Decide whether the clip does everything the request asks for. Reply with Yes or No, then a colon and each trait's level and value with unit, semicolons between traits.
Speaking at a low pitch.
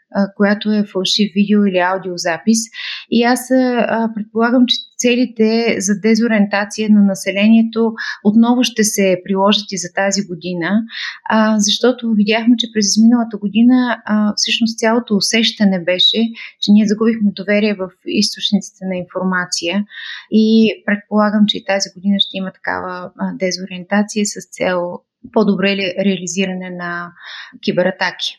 No: high, 210 Hz